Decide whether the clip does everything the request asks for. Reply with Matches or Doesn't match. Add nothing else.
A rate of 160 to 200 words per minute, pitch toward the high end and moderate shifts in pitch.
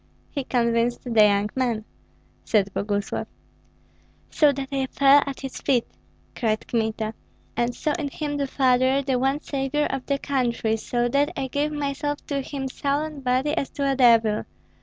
Matches